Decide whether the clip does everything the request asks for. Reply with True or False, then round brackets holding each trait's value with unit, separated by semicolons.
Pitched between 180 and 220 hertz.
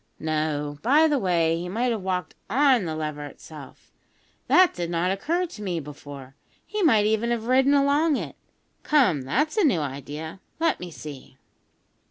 True (185 Hz)